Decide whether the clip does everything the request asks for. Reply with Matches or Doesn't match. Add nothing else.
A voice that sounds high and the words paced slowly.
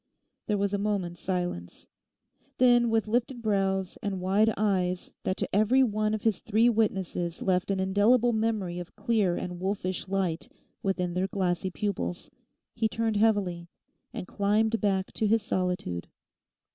Doesn't match